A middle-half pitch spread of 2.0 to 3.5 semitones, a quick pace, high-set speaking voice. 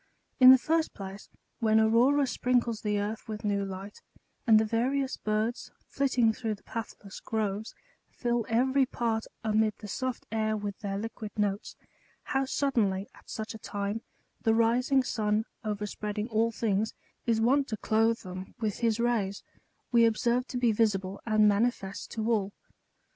No: narrow, 2.4 semitones; average, 160 wpm; high, 220 Hz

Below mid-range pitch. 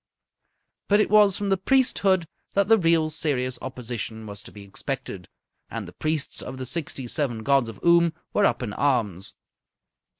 No: medium, 145 Hz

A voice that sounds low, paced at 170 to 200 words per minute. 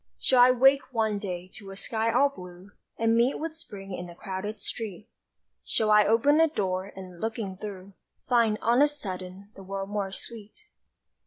No: high, 210 Hz; average, 180 wpm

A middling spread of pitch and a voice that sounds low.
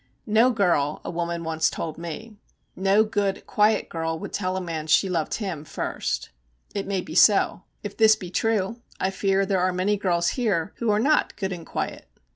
No: average, 3.6 semitones; high, 190 Hz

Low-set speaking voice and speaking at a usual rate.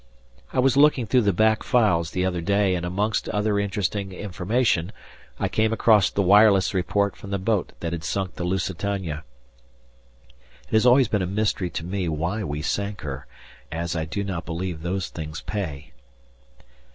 Yes: very low, 95 Hz; average, 175 wpm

